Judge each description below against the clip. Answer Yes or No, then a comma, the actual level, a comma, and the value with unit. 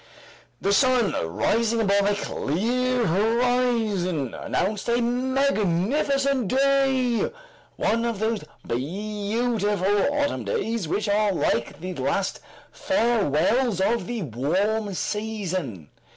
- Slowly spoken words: Yes, slow, 100 wpm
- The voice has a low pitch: No, high, 215 Hz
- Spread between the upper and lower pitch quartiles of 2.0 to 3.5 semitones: No, average, 4.4 semitones